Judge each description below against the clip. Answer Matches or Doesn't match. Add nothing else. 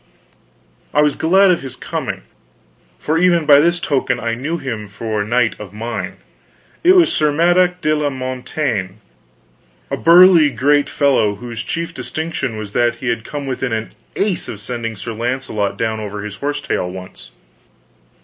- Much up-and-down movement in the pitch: Matches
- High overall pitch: Doesn't match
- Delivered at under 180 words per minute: Matches